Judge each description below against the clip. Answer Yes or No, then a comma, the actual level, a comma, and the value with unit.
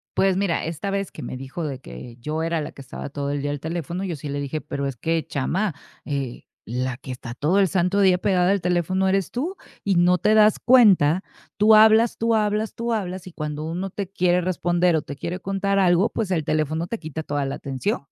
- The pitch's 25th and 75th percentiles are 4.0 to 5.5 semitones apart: Yes, average, 5.1 semitones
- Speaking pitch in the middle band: Yes, medium, 175 Hz